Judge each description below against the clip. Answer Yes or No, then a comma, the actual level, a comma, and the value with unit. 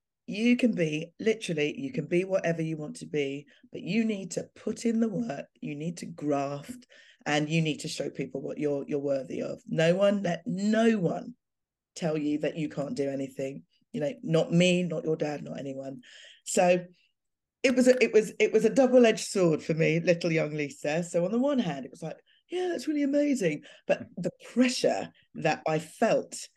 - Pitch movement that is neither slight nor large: No, wide, 7.0 semitones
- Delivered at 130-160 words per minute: No, fast, 205 wpm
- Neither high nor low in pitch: Yes, medium, 175 Hz